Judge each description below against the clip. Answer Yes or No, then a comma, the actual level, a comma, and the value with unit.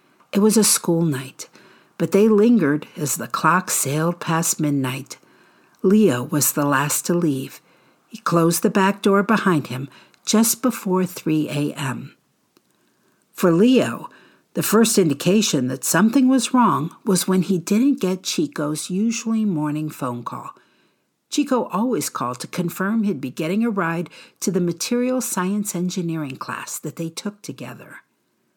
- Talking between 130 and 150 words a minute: Yes, average, 145 wpm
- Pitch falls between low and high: Yes, medium, 180 Hz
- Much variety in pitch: Yes, wide, 5.7 semitones